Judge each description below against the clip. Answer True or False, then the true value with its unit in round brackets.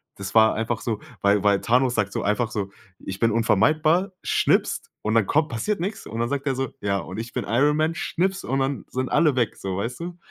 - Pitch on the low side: True (120 Hz)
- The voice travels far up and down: True (5.9 semitones)